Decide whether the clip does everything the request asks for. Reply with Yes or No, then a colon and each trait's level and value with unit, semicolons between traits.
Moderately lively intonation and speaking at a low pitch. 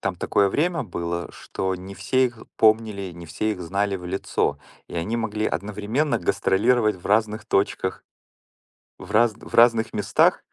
Yes: average, 3.0 semitones; low, 105 Hz